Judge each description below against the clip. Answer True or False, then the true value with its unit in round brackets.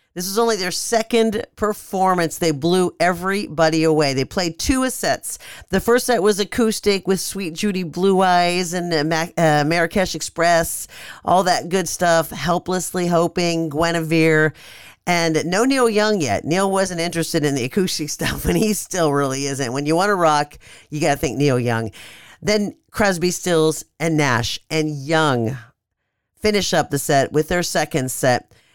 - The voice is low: False (170 Hz)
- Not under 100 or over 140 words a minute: False (165 wpm)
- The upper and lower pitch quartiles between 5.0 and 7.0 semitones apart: False (3.9 semitones)